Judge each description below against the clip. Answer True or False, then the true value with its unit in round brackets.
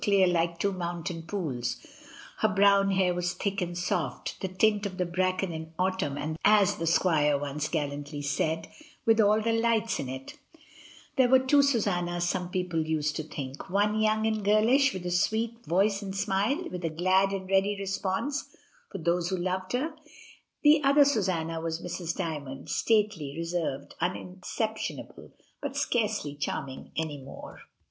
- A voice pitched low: False (185 Hz)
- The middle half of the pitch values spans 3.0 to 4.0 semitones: False (4.4 semitones)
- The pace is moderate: True (170 wpm)